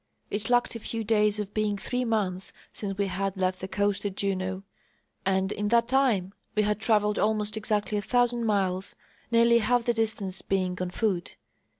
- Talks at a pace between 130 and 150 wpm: No, average, 185 wpm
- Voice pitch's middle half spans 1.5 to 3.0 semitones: Yes, average, 2.7 semitones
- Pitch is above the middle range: Yes, high, 210 Hz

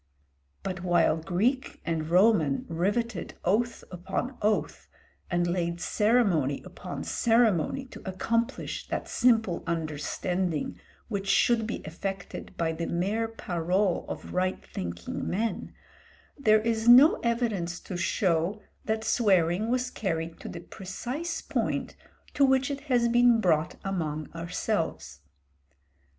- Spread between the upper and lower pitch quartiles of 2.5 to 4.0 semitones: No, average, 5.3 semitones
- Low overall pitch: No, high, 195 Hz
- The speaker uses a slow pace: Yes, slow, 120 wpm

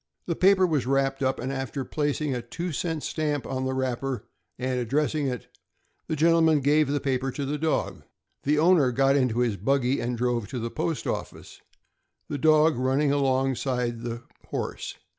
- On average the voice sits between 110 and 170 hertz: Yes, low, 135 Hz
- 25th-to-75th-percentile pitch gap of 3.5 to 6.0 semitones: No, average, 3.1 semitones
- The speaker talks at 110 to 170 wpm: No, average, 180 wpm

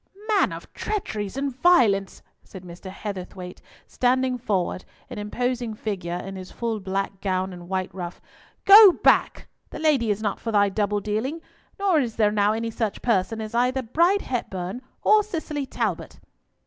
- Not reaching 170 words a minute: Yes, average, 160 wpm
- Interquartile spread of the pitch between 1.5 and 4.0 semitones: No, average, 5.1 semitones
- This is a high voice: Yes, high, 215 Hz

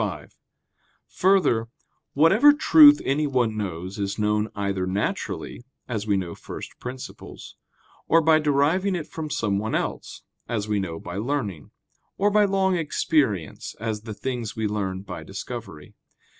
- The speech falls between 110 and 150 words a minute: Yes, average, 140 wpm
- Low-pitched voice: Yes, low, 115 Hz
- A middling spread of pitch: No, wide, 7.7 semitones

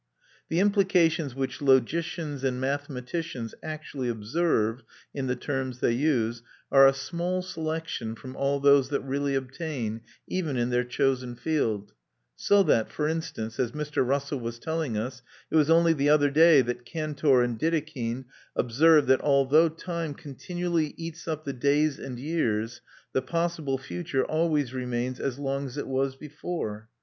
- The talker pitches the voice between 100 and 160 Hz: Yes, medium, 140 Hz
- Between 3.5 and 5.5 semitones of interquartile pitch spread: Yes, average, 4.1 semitones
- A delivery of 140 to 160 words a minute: Yes, average, 155 wpm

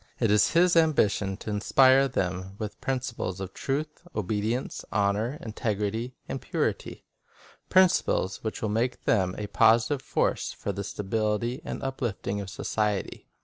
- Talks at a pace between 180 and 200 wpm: No, average, 145 wpm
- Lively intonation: No, average, 4.3 semitones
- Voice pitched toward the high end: No, low, 110 Hz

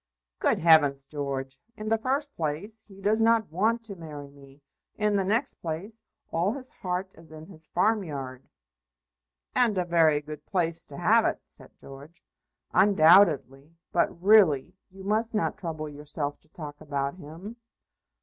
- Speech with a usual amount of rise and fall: No, wide, 5.8 semitones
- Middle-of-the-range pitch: Yes, medium, 165 Hz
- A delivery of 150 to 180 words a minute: Yes, average, 155 wpm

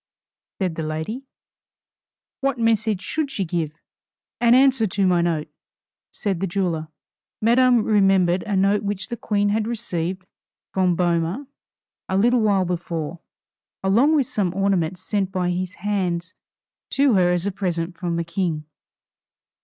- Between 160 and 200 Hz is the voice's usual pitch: Yes, high, 190 Hz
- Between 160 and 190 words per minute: No, average, 145 wpm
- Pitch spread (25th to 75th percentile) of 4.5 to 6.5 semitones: No, average, 3.7 semitones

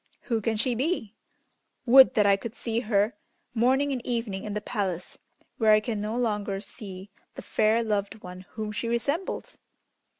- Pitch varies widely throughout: No, narrow, 2.6 semitones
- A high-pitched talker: Yes, high, 220 Hz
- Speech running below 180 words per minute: Yes, average, 170 wpm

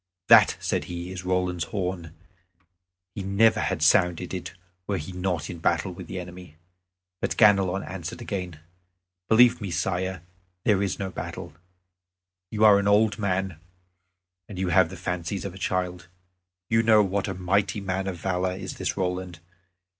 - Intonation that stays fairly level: Yes, narrow, 1.8 semitones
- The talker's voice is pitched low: Yes, very low, 95 Hz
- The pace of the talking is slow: No, average, 160 wpm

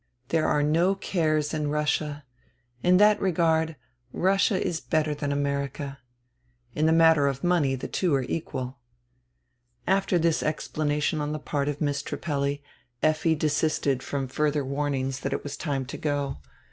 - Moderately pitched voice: Yes, medium, 150 Hz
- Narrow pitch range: Yes, narrow, 2.3 semitones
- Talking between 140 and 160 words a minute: Yes, average, 155 wpm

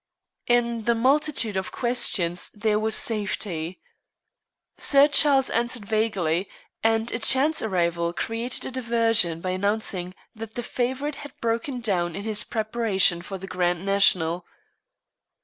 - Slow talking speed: Yes, slow, 130 wpm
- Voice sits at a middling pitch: No, high, 220 Hz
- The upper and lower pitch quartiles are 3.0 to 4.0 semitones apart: No, average, 4.4 semitones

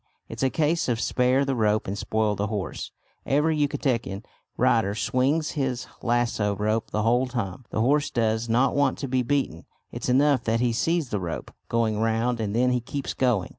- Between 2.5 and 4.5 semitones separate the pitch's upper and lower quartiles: Yes, average, 3.5 semitones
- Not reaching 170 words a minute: No, average, 190 wpm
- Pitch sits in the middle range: No, low, 120 Hz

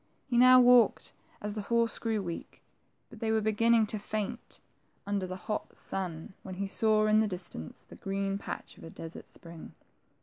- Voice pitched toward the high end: Yes, high, 210 Hz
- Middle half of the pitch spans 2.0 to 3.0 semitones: Yes, narrow, 2.6 semitones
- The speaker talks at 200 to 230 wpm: Yes, fast, 205 wpm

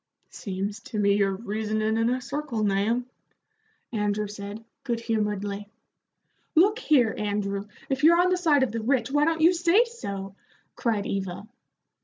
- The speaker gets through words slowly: No, average, 155 wpm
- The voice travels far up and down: Yes, wide, 5.7 semitones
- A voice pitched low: No, high, 220 Hz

